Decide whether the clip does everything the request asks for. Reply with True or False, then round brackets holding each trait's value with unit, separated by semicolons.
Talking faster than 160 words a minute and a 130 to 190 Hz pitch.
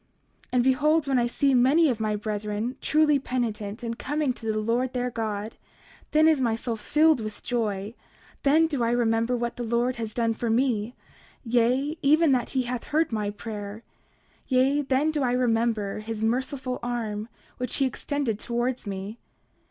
False (175 wpm; 240 Hz)